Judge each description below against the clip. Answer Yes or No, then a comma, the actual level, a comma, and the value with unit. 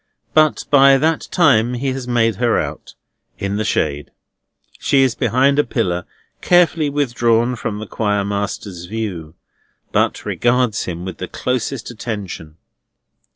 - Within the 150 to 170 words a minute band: No, average, 140 wpm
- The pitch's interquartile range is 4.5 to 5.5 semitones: Yes, average, 4.8 semitones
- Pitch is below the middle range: Yes, low, 115 Hz